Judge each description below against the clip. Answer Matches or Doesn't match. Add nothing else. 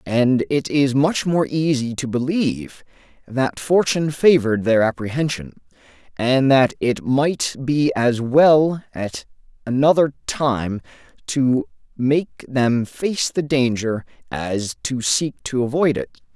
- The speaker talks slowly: Matches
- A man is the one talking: Matches